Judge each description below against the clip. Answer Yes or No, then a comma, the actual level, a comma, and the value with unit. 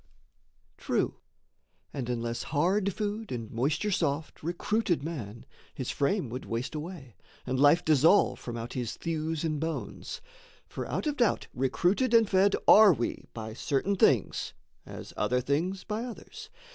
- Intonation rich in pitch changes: Yes, wide, 7.7 semitones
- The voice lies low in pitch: No, medium, 160 Hz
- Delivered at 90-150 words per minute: Yes, average, 145 wpm